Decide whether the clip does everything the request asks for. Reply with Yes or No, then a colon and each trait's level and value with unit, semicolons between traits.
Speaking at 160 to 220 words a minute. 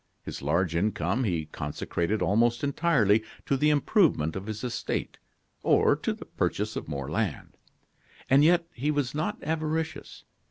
No: average, 150 wpm